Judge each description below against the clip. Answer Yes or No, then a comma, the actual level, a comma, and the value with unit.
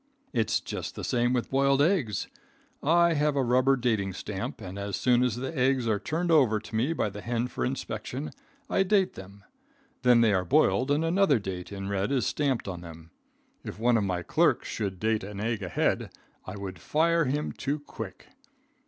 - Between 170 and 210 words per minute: Yes, average, 195 wpm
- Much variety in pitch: Yes, wide, 5.8 semitones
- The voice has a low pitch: Yes, low, 120 Hz